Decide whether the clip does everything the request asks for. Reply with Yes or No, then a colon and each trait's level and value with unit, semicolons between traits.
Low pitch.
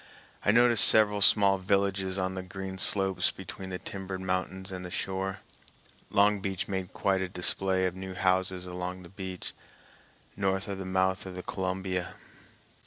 Yes: very low, 95 Hz